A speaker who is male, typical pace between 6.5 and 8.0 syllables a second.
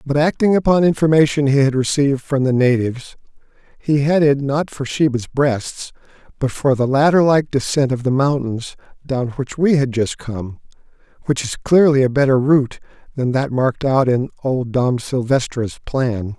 No: male; 4.9 syllables/s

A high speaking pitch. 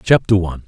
No: low, 100 Hz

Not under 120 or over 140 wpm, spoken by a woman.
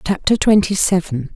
Yes: slow, 135 wpm; female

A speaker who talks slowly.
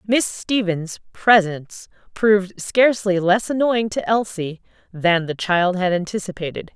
Yes: slow, 125 wpm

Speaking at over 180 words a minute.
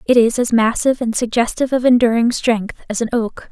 Yes: fast, 205 wpm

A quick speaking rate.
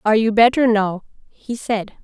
No: average, 175 wpm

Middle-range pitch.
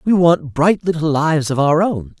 Yes: medium, 155 Hz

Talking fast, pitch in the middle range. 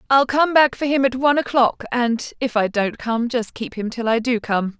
No: fast, 250 wpm; high, 240 Hz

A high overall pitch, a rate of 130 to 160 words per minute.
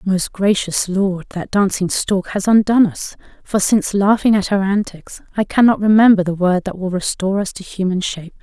No: high, 195 Hz; average, 190 wpm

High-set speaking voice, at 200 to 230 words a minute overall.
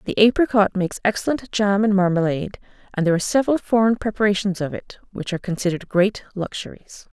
No: high, 200 Hz; average, 165 wpm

